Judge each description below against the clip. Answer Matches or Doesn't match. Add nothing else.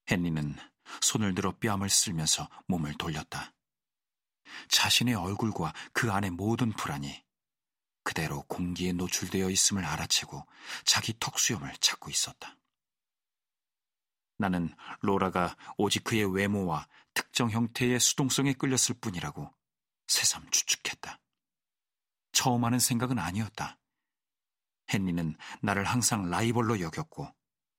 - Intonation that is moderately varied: Matches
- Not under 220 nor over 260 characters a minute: Matches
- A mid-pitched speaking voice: Doesn't match